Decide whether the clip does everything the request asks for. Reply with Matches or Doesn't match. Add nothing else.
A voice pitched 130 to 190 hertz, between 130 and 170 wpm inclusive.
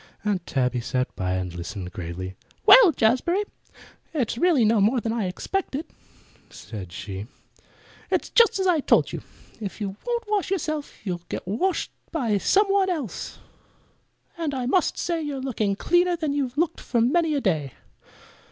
Doesn't match